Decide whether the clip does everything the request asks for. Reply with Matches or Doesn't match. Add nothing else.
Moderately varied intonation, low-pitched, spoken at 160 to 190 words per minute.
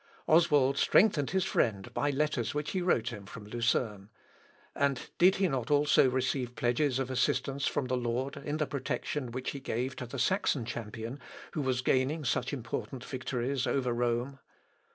Matches